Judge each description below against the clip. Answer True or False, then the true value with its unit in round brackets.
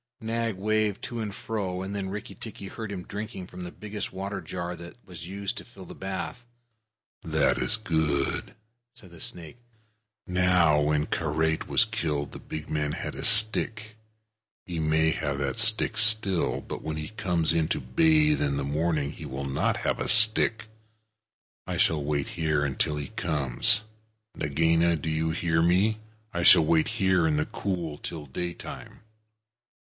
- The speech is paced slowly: False (170 wpm)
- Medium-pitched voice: False (85 Hz)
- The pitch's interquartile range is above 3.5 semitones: True (5.1 semitones)